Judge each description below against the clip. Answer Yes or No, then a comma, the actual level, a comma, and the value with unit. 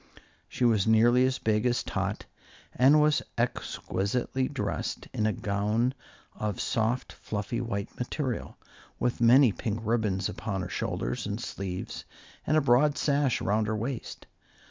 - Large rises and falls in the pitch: No, average, 3.3 semitones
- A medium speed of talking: Yes, average, 145 wpm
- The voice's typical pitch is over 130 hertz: No, low, 115 Hz